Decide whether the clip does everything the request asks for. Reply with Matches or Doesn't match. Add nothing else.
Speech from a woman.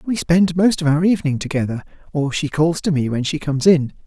Doesn't match